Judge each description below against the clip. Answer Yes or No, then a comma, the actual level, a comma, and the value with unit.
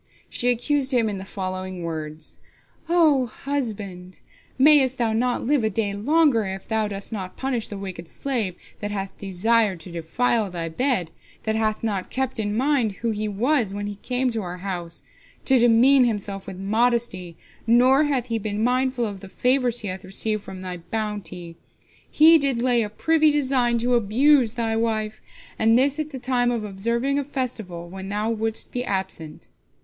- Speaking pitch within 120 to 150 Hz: No, high, 225 Hz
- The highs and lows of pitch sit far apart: No, average, 4.5 semitones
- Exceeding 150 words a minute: Yes, average, 180 wpm